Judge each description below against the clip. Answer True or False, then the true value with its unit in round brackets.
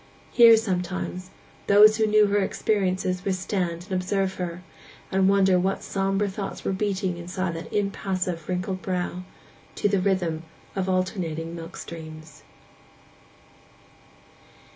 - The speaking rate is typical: False (130 wpm)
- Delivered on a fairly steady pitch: True (1.7 semitones)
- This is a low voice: False (185 Hz)